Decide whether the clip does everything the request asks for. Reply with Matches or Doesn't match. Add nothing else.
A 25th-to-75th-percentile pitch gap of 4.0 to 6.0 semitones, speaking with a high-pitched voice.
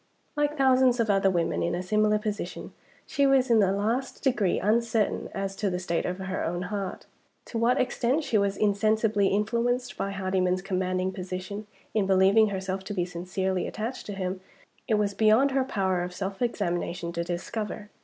Doesn't match